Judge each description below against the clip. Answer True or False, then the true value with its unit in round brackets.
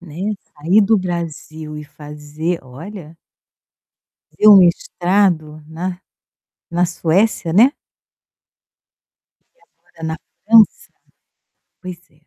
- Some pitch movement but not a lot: True (3.6 semitones)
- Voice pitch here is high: False (175 Hz)